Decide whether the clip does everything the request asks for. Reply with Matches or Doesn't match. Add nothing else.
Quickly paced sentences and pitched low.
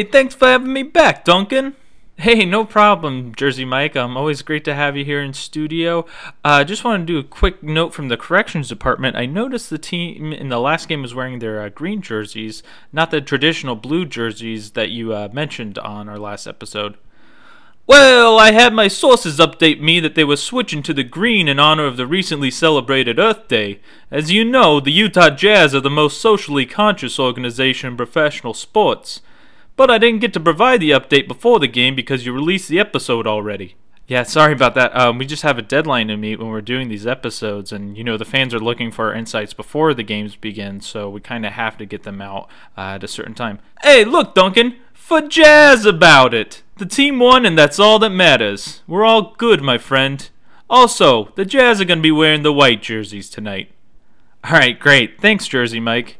Doesn't match